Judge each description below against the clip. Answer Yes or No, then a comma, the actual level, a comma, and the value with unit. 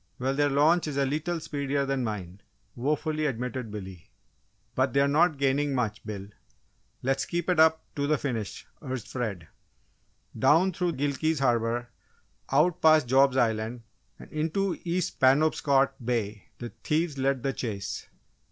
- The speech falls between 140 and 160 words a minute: Yes, average, 150 wpm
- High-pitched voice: No, low, 135 Hz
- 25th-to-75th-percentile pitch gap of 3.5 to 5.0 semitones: Yes, average, 4.1 semitones